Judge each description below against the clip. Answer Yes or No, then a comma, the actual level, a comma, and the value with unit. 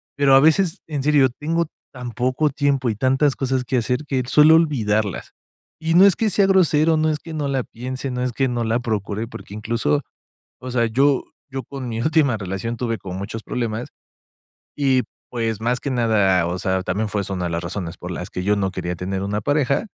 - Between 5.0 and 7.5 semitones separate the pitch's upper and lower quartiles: Yes, wide, 5.4 semitones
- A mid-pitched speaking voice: No, low, 125 Hz